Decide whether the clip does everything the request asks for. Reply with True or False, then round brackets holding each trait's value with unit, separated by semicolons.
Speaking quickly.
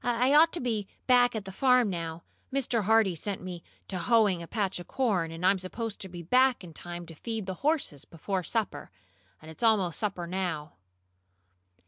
False (195 wpm)